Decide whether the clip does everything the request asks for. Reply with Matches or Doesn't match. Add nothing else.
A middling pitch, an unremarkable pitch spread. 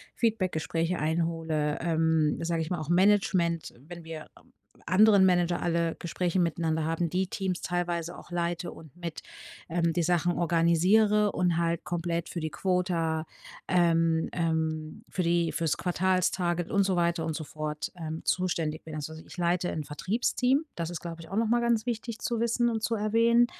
Doesn't match